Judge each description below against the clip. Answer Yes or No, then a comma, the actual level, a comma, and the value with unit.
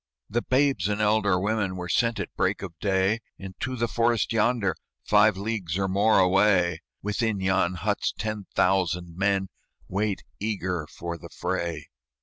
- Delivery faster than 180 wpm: No, average, 150 wpm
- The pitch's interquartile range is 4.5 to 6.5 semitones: No, average, 2.8 semitones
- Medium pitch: No, low, 100 Hz